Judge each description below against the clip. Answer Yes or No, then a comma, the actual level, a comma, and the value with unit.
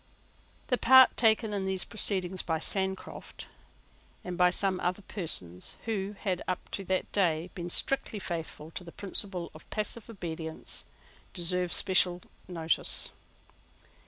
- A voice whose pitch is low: No, medium, 185 Hz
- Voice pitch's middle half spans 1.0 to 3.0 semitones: Yes, average, 2.7 semitones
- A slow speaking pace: Yes, slow, 130 wpm